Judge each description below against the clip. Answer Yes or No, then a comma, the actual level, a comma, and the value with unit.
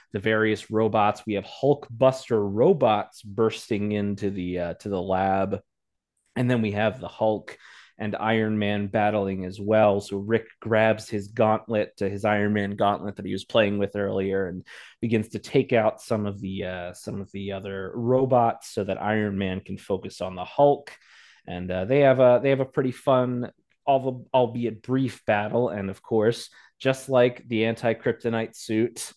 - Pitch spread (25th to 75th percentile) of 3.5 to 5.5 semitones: No, average, 3.1 semitones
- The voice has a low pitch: Yes, low, 105 Hz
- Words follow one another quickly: No, average, 180 wpm